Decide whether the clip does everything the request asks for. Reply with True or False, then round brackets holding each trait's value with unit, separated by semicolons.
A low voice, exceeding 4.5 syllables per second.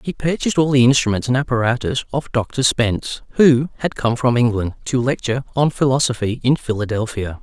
True (125 Hz; 5.6 syllables/s)